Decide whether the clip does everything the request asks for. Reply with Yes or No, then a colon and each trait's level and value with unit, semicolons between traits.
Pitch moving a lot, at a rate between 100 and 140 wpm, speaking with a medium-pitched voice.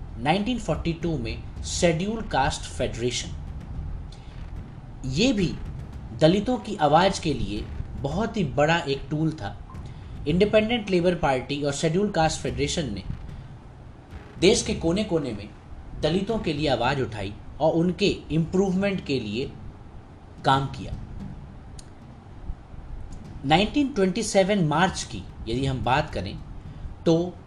Yes: wide, 8.5 semitones; slow, 110 wpm; medium, 150 Hz